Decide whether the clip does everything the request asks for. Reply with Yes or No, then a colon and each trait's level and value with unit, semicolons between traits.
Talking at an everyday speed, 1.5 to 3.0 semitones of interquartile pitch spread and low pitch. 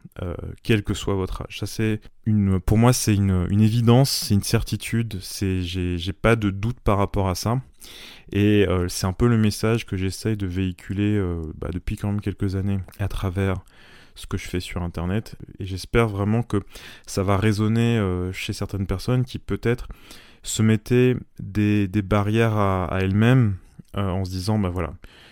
Yes: average, 195 wpm; narrow, 2.6 semitones; low, 100 Hz